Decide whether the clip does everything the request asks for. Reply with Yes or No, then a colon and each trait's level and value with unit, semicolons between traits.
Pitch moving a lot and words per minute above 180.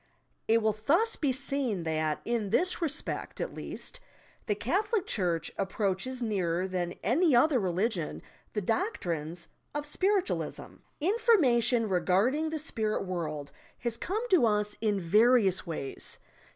No: wide, 8.1 semitones; slow, 135 wpm